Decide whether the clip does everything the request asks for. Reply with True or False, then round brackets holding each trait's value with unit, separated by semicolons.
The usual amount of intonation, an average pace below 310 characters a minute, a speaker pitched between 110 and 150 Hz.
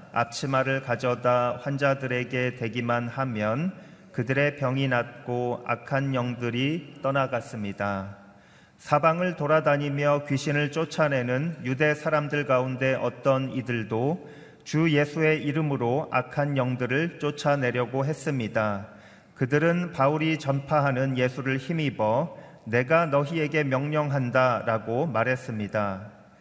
True (3.4 semitones; 270 characters per minute; 135 Hz)